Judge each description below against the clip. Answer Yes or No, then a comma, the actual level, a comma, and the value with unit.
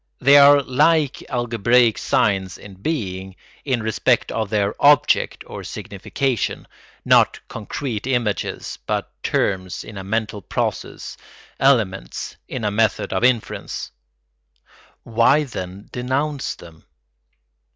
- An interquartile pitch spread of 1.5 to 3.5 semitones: No, average, 5.0 semitones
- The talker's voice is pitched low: Yes, low, 115 Hz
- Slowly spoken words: Yes, slow, 110 wpm